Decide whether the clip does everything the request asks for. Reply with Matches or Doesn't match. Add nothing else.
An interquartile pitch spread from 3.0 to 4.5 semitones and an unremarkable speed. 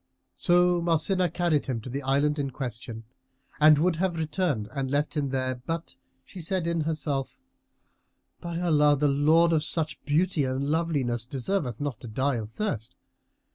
Matches